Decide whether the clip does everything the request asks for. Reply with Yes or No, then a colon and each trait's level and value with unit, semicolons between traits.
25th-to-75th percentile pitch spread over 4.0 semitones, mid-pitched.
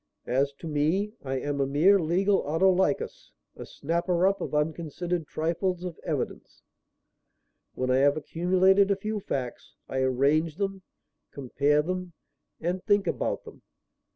Yes: average, 4.6 semitones; medium, 170 Hz